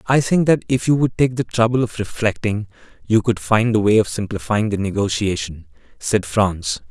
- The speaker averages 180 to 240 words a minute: Yes, average, 190 wpm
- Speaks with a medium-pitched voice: No, low, 110 Hz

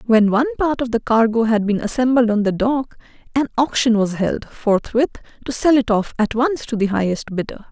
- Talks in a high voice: Yes, high, 235 Hz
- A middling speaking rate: No, fast, 210 wpm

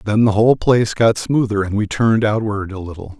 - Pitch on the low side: Yes, low, 105 Hz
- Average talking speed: No, fast, 225 wpm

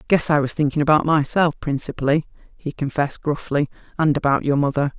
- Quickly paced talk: No, average, 170 wpm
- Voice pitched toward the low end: No, medium, 145 Hz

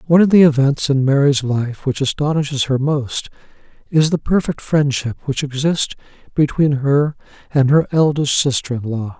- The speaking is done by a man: Yes, male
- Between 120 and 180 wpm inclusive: Yes, average, 165 wpm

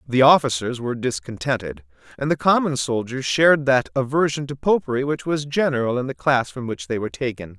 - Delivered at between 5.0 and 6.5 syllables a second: Yes, 5.8 syllables/s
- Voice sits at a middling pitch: No, low, 130 Hz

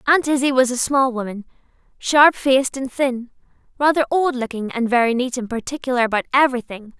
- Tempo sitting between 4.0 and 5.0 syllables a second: No, 5.9 syllables/s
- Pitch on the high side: Yes, very high, 255 Hz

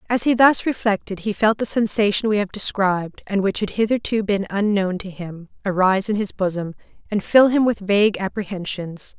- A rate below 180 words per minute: No, average, 190 wpm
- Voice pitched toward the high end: Yes, high, 205 Hz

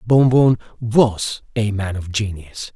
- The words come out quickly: No, average, 155 wpm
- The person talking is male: Yes, male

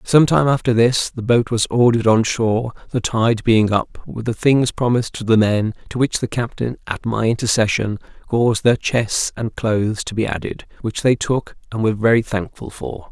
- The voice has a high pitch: No, low, 115 Hz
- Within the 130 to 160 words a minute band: No, average, 200 wpm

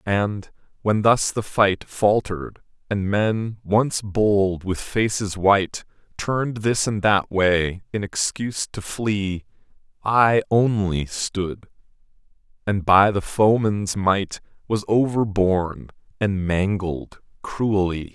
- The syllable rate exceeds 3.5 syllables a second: No, 3.4 syllables/s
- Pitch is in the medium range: No, low, 100 Hz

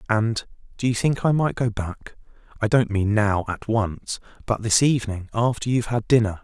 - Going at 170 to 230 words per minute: Yes, average, 185 wpm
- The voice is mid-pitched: No, low, 110 Hz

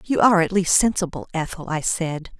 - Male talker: No, female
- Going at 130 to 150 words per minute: No, average, 200 wpm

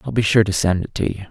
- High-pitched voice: No, low, 100 Hz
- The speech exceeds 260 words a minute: Yes, fast, 365 wpm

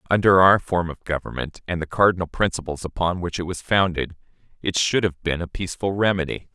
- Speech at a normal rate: Yes, average, 190 wpm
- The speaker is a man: Yes, male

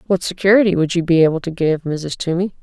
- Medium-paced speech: No, fast, 230 wpm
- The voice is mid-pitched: Yes, medium, 175 Hz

